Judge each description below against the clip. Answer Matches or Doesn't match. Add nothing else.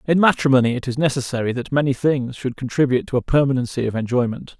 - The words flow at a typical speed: Matches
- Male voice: Matches